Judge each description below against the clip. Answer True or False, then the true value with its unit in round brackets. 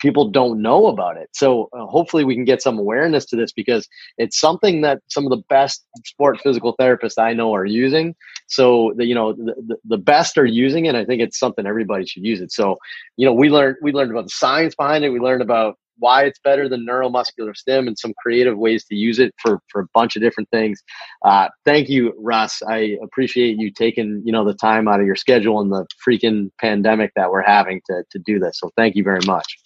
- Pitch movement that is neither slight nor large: True (3.3 semitones)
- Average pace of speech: False (235 wpm)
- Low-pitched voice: True (115 Hz)